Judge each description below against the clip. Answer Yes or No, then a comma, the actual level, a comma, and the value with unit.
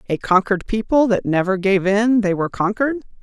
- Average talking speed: Yes, average, 185 wpm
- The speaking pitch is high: Yes, high, 205 Hz